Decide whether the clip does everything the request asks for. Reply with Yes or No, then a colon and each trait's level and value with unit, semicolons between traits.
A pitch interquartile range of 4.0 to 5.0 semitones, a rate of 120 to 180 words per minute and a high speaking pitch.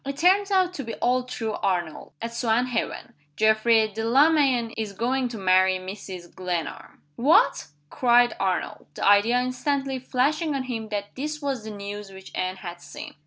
Yes: average, 4.7 semitones; average, 165 wpm; high, 230 Hz